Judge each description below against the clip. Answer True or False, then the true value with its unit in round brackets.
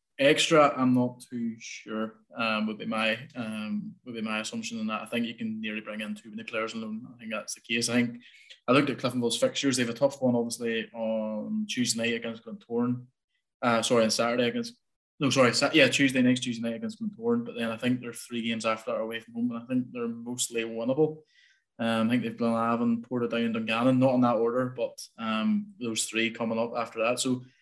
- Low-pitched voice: True (120 Hz)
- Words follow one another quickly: True (230 wpm)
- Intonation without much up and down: True (2.1 semitones)